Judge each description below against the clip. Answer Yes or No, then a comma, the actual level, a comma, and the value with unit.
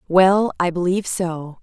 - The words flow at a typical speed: Yes, average, 150 wpm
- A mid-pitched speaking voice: Yes, medium, 180 Hz